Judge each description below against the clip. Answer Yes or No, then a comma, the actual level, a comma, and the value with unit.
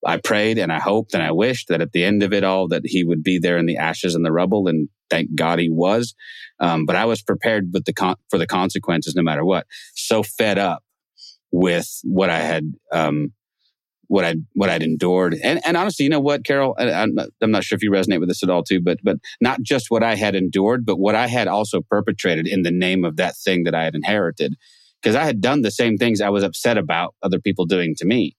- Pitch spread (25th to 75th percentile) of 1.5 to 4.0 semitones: Yes, average, 3.5 semitones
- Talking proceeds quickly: Yes, fast, 250 wpm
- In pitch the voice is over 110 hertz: No, very low, 95 Hz